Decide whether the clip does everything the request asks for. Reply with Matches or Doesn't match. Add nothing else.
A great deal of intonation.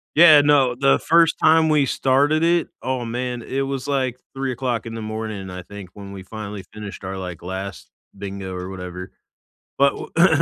Matches